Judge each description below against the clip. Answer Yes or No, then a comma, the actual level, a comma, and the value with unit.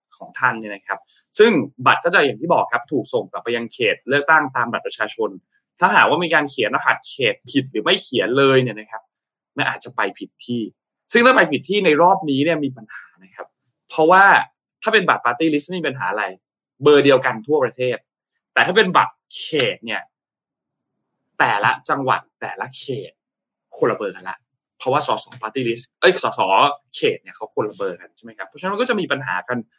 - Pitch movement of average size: No, wide, 7.2 semitones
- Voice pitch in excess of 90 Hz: Yes, low, 135 Hz